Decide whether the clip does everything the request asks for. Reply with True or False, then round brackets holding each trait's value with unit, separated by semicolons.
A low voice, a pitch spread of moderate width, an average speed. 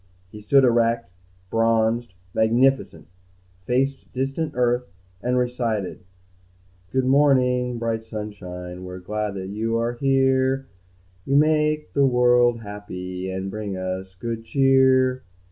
False (120 Hz; 4.2 semitones; 110 wpm)